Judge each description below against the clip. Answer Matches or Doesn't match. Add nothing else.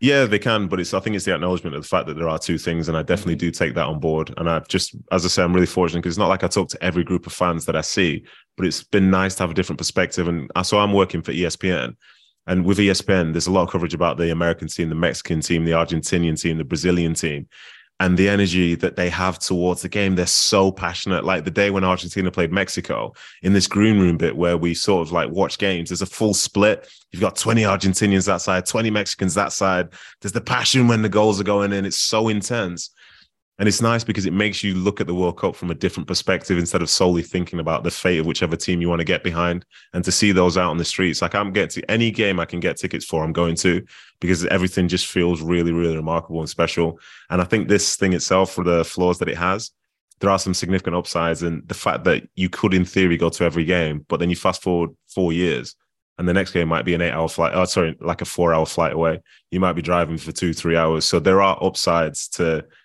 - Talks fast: Matches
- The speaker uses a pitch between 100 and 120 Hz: Doesn't match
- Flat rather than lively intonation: Matches